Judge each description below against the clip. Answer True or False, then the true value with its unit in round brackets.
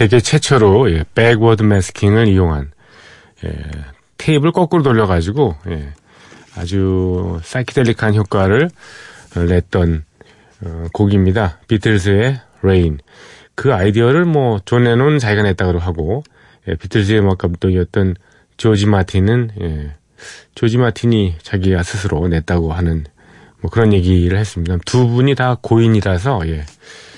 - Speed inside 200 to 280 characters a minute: True (270 characters per minute)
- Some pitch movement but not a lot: True (4.7 semitones)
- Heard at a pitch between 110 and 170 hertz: False (100 Hz)